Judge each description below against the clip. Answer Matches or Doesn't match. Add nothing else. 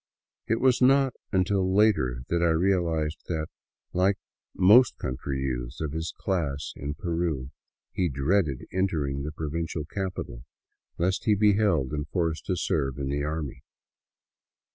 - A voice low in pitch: Matches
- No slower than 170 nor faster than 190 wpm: Doesn't match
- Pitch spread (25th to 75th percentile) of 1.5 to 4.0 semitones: Doesn't match